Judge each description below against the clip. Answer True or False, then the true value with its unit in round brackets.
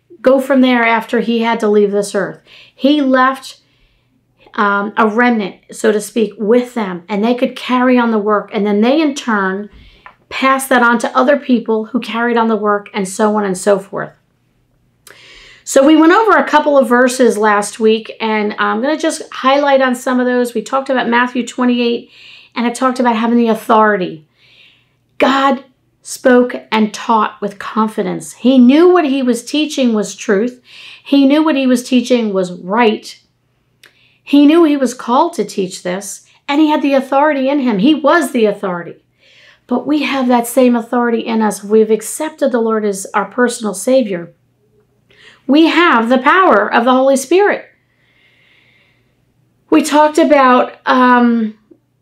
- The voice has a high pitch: True (240 Hz)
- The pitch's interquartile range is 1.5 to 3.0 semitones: False (4.1 semitones)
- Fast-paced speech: False (175 wpm)